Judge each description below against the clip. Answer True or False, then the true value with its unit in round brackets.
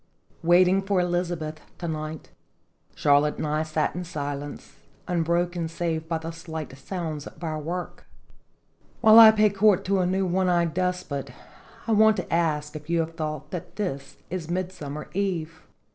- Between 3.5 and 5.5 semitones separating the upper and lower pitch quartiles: False (2.9 semitones)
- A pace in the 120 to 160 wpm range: False (175 wpm)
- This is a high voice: False (170 Hz)